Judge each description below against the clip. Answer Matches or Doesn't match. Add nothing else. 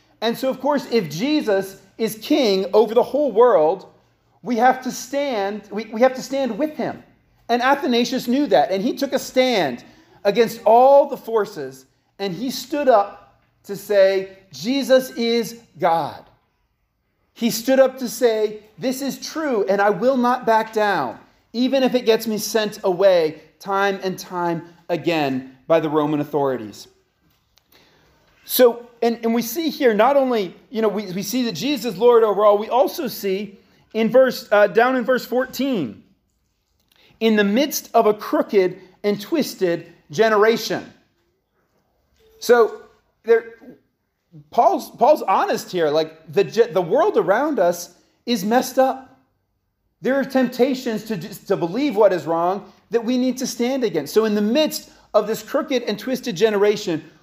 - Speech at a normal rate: Matches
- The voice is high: Matches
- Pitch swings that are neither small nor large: Matches